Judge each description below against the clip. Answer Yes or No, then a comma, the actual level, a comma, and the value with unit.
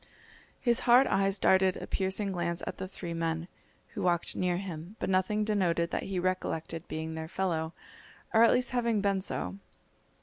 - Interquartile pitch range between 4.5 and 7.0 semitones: No, average, 3.0 semitones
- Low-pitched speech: No, medium, 185 Hz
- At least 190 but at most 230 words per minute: No, average, 175 wpm